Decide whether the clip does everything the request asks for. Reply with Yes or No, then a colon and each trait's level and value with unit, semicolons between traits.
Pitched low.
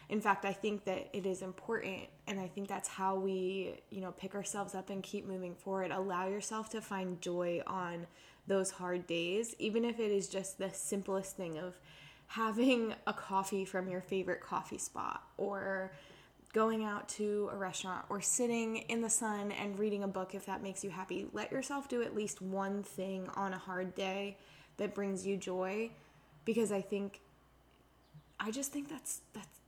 No: high, 195 Hz